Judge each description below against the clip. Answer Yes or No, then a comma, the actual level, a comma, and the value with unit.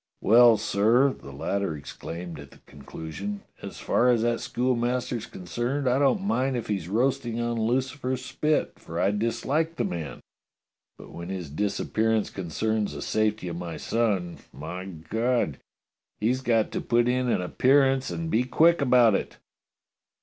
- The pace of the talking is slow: No, average, 155 wpm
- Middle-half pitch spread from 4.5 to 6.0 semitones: Yes, average, 5.1 semitones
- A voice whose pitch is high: No, low, 115 Hz